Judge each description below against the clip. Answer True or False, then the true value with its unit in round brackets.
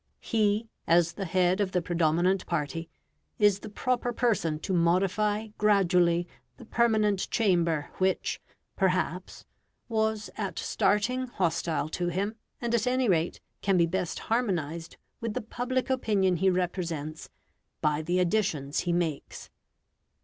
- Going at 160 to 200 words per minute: False (135 wpm)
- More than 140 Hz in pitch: True (185 Hz)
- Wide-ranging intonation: False (4.1 semitones)